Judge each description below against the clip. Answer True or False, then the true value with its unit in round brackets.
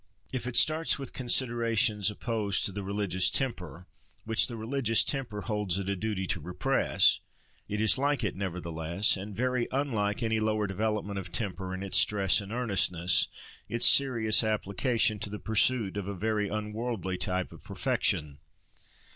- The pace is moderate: True (160 wpm)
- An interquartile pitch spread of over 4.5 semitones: False (3.3 semitones)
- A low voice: True (105 Hz)